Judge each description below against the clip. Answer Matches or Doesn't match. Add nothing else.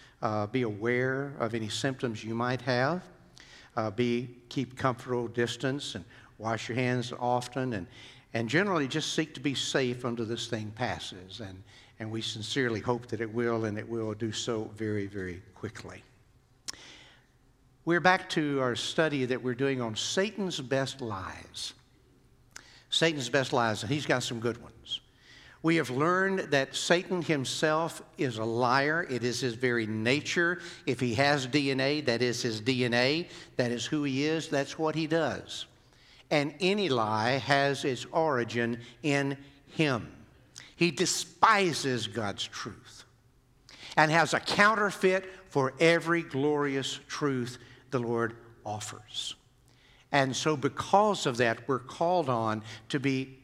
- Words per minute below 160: Matches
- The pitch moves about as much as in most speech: Matches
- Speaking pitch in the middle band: Doesn't match